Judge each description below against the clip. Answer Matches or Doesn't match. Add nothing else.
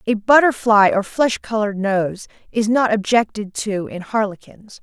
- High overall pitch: Matches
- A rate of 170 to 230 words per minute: Doesn't match